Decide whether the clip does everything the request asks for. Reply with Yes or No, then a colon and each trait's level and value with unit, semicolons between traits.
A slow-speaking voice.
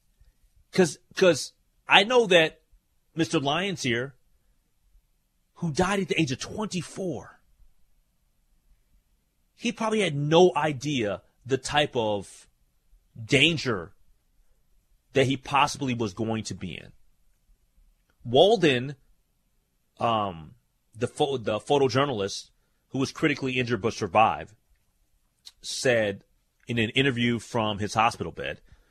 Yes: slow, 105 wpm